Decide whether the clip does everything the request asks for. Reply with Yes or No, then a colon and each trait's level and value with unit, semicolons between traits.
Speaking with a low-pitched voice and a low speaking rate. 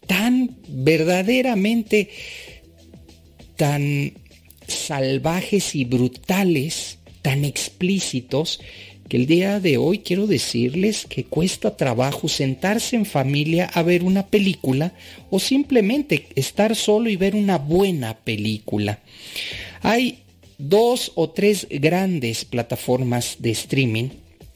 No: medium, 155 Hz; slow, 105 wpm